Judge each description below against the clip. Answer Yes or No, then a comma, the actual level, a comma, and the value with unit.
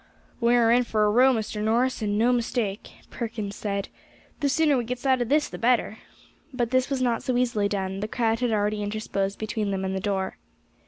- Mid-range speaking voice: No, high, 225 Hz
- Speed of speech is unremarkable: No, fast, 215 wpm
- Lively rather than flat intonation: No, average, 3.2 semitones